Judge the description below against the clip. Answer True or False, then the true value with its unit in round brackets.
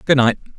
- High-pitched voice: False (130 Hz)